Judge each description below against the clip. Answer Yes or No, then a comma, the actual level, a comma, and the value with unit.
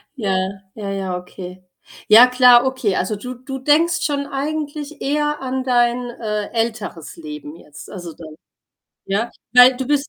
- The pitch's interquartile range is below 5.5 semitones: No, wide, 5.8 semitones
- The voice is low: No, high, 240 Hz